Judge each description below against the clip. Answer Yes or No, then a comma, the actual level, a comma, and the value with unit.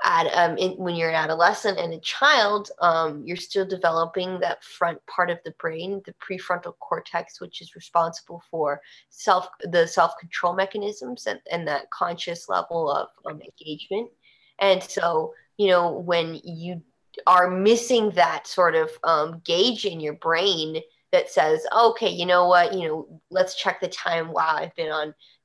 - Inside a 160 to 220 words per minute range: Yes, average, 170 wpm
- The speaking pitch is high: No, medium, 175 Hz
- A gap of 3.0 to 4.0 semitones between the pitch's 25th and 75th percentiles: No, narrow, 2.5 semitones